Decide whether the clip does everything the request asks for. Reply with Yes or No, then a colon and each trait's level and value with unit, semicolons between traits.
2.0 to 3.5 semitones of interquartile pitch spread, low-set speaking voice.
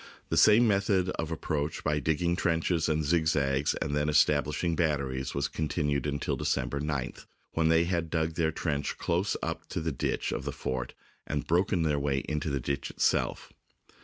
Yes: narrow, 2.6 semitones; very low, 80 Hz